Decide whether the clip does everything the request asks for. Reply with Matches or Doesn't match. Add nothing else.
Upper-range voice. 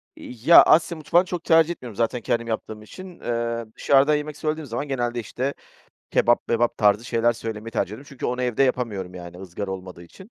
Doesn't match